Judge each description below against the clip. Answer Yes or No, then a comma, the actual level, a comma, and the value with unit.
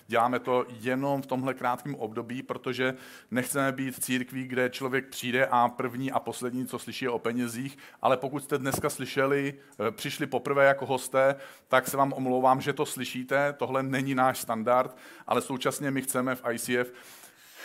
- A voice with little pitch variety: Yes, narrow, 1.4 semitones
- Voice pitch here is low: Yes, low, 130 Hz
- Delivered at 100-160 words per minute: No, fast, 170 wpm